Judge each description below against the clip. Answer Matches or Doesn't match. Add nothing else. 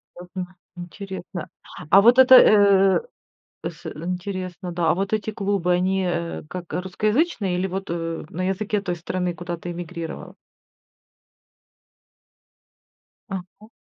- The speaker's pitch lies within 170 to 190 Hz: Matches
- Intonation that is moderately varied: Doesn't match